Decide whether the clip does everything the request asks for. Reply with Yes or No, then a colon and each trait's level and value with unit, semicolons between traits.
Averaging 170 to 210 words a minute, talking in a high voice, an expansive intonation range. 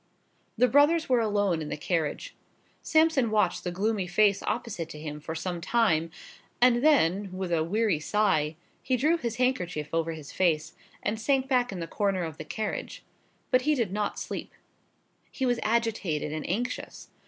Yes: average, 175 wpm; high, 205 Hz; wide, 6.7 semitones